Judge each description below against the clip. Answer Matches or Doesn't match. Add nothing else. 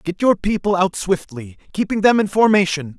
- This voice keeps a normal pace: Matches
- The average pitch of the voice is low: Doesn't match